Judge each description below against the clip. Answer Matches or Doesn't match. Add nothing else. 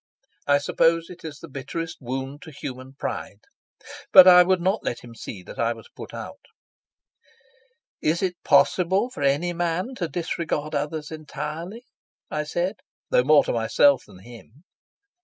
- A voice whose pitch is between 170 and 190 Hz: Doesn't match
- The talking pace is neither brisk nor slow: Matches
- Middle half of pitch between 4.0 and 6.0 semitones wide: Matches